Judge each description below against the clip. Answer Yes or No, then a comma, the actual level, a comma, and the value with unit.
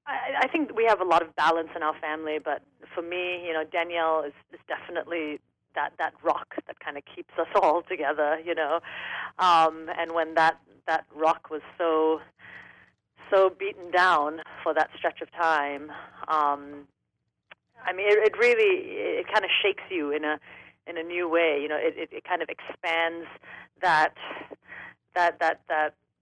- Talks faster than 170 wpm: Yes, average, 180 wpm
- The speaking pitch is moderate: Yes, medium, 165 Hz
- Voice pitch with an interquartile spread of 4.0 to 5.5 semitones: No, narrow, 2.5 semitones